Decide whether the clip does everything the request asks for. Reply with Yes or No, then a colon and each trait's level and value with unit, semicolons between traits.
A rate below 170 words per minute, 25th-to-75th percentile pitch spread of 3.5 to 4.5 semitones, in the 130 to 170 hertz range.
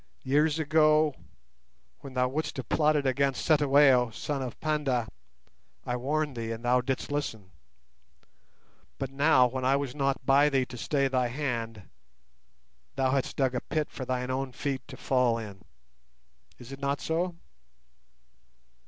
No: average, 150 wpm; narrow, 2.6 semitones; low, 135 Hz